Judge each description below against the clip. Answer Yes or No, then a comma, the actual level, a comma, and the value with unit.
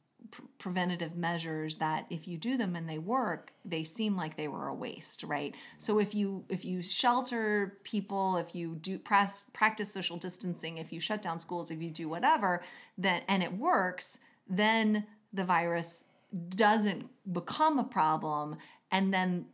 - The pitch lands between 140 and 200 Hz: Yes, medium, 185 Hz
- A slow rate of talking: No, average, 165 wpm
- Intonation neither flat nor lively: Yes, average, 3.7 semitones